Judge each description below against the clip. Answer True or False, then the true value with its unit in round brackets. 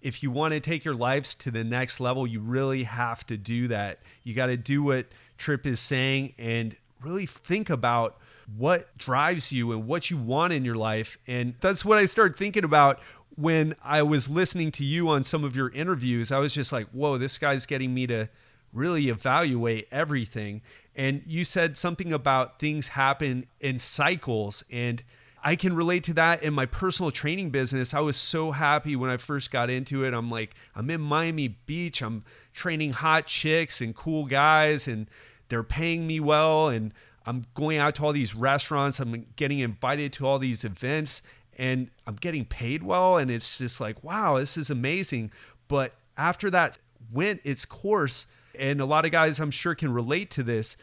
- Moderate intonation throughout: True (4.3 semitones)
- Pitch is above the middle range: False (135 Hz)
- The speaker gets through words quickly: False (190 wpm)